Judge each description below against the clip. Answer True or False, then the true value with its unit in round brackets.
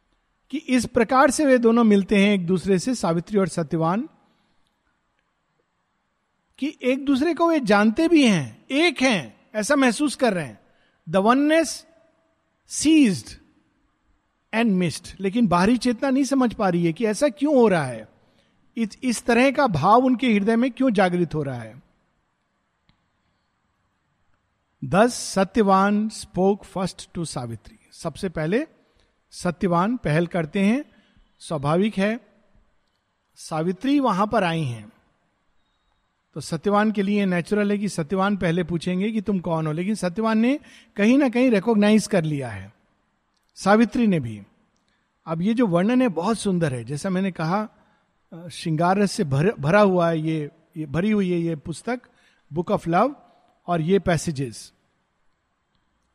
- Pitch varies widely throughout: True (6.0 semitones)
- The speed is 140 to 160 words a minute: True (145 wpm)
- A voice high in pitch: True (205 Hz)